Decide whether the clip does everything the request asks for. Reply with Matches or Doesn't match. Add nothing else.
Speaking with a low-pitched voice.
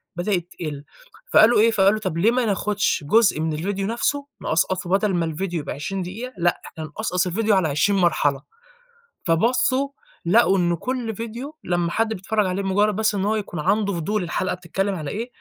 Doesn't match